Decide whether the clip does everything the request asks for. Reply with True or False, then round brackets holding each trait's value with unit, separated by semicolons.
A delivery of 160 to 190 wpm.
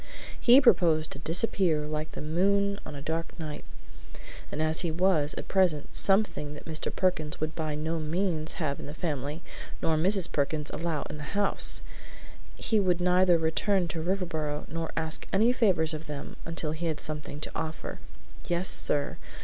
True (175 wpm)